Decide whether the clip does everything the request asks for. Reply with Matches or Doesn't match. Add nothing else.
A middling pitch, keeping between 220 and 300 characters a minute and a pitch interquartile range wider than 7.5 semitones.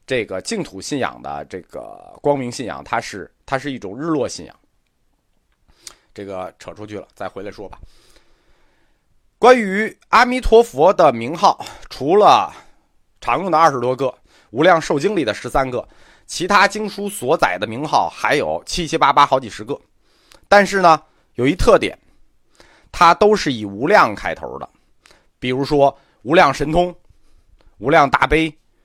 Matches